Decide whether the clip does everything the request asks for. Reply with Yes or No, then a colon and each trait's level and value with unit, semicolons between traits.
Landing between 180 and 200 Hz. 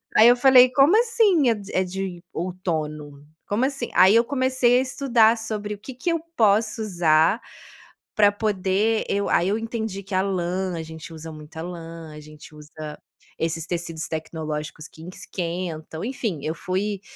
Yes: high, 190 Hz